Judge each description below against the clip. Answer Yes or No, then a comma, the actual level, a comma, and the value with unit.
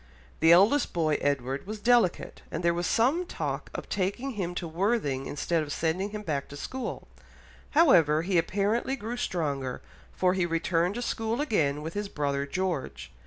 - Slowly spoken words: No, average, 170 wpm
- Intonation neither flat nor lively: No, wide, 5.8 semitones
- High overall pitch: No, medium, 180 Hz